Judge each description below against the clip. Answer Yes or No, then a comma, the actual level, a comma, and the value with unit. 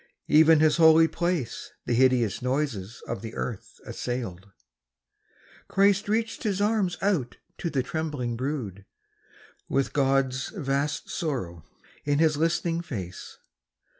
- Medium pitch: Yes, medium, 145 Hz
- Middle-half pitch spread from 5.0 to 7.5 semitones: Yes, wide, 5.4 semitones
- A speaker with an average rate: No, slow, 120 wpm